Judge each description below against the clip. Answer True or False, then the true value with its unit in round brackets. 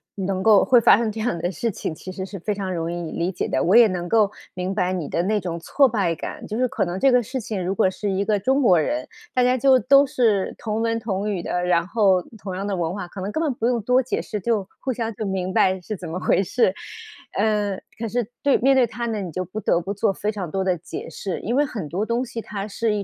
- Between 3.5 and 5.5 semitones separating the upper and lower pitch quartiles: True (3.8 semitones)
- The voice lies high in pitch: True (205 Hz)